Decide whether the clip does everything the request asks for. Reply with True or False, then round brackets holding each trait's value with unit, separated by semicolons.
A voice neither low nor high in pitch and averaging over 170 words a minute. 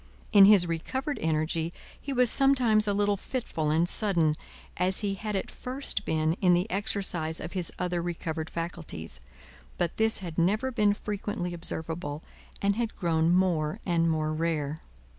False (175 Hz; 160 wpm)